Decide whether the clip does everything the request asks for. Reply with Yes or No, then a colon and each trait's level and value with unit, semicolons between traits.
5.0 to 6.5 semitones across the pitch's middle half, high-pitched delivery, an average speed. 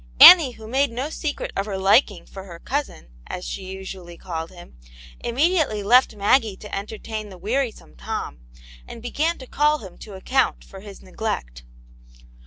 Yes: wide, 5.5 semitones; high, 210 Hz; average, 170 wpm